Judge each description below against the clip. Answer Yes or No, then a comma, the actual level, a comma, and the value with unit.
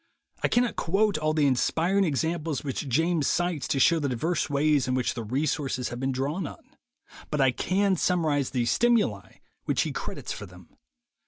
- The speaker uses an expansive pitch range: No, average, 4.5 semitones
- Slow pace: No, average, 180 wpm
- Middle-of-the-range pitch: Yes, medium, 150 Hz